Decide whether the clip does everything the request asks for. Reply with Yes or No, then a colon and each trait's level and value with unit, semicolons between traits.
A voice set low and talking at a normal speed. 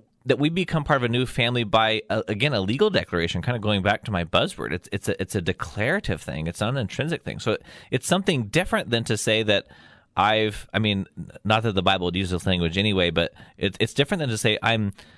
No: low, 110 Hz; fast, 245 wpm